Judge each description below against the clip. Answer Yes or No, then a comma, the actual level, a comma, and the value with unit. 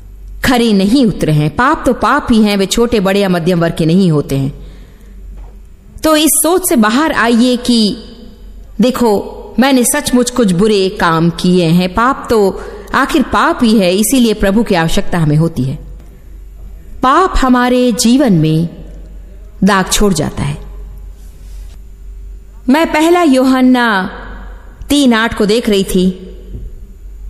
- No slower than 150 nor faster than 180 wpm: No, average, 140 wpm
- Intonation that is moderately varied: No, wide, 7.3 semitones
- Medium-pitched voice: No, high, 205 Hz